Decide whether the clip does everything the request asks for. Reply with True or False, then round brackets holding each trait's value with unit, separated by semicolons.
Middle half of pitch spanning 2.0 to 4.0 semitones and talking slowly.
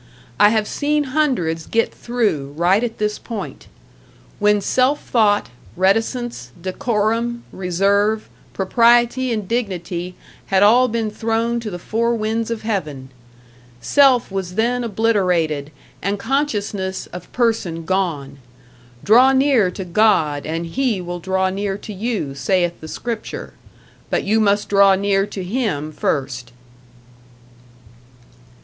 False (4.4 semitones; 125 wpm)